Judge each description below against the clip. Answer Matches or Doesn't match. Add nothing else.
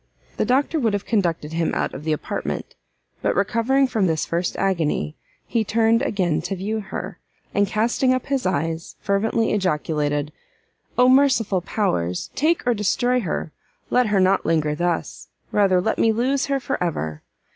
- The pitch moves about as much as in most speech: Doesn't match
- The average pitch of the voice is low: Doesn't match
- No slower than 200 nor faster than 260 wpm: Doesn't match